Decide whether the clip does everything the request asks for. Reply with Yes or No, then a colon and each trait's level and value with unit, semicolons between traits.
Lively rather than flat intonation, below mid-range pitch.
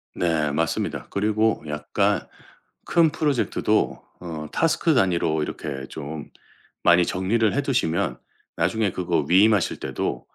Yes: wide, 6.1 semitones; very low, 90 Hz